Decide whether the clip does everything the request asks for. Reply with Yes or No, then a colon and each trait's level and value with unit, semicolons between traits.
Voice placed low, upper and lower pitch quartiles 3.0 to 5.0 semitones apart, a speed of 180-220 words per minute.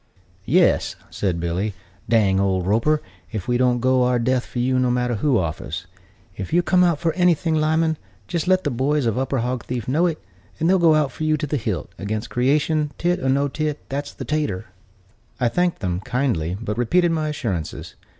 No: low, 130 Hz; wide, 5.6 semitones; average, 200 wpm